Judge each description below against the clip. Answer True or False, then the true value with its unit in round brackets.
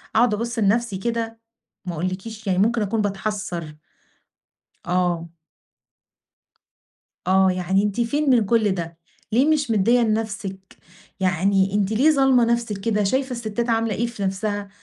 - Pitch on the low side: False (210 Hz)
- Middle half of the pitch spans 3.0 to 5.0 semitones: True (3.5 semitones)